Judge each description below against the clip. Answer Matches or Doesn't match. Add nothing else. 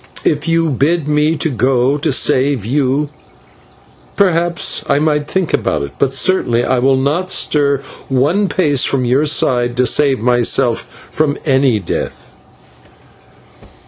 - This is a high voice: Doesn't match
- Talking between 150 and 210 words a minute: Doesn't match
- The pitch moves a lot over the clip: Doesn't match